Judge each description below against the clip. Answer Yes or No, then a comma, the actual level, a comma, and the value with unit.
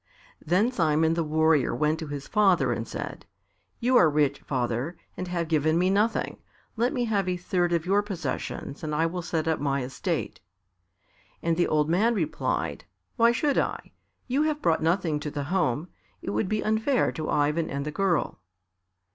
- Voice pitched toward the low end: No, medium, 165 Hz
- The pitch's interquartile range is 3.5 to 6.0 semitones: Yes, average, 4.6 semitones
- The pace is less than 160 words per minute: No, average, 180 wpm